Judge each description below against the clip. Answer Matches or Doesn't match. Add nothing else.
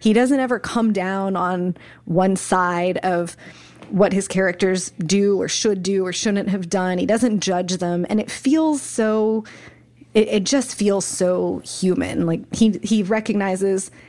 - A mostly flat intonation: Doesn't match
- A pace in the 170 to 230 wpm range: Doesn't match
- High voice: Matches